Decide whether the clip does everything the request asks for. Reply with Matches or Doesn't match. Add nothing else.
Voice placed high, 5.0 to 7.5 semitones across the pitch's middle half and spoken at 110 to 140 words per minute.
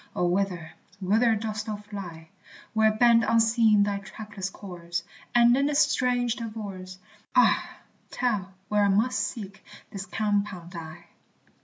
Doesn't match